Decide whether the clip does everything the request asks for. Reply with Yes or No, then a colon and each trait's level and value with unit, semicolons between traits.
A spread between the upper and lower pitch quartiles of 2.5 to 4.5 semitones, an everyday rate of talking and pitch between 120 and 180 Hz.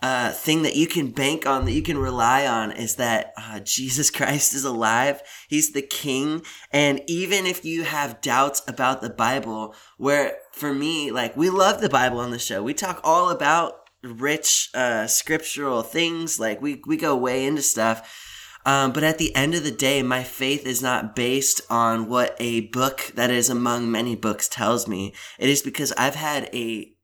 Yes: average, 3.9 semitones; average, 195 wpm; low, 135 Hz